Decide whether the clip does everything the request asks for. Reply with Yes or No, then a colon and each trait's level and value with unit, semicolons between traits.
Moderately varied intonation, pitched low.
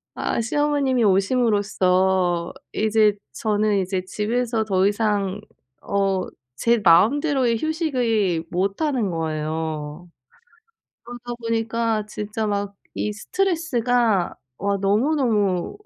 No: average, 4.1 semitones; high, 210 Hz